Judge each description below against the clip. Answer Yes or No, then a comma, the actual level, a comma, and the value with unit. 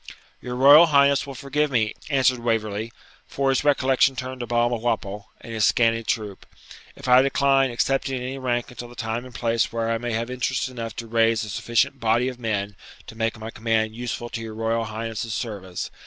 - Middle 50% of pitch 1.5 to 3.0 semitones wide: Yes, narrow, 2.5 semitones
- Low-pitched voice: Yes, low, 120 Hz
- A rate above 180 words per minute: Yes, average, 195 wpm